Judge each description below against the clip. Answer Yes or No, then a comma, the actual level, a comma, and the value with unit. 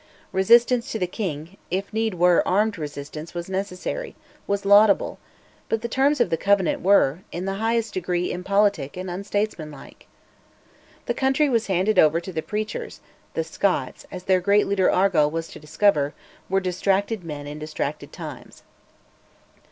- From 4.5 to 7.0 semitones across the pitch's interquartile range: No, average, 3.7 semitones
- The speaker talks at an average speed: Yes, average, 155 wpm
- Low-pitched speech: No, high, 190 Hz